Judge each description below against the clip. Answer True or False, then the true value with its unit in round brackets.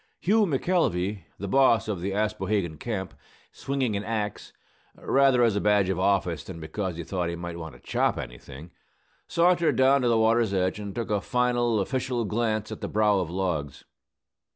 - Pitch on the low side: True (105 Hz)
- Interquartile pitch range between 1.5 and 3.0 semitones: False (4.7 semitones)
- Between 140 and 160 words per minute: False (180 wpm)